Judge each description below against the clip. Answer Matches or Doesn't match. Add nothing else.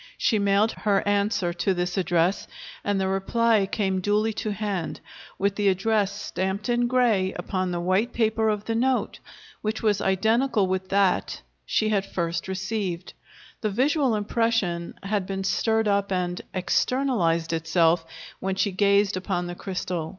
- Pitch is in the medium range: Doesn't match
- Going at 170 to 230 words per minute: Doesn't match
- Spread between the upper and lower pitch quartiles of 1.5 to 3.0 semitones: Matches